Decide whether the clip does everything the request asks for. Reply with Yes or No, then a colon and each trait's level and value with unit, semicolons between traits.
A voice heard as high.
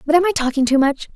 Yes: very high, 300 Hz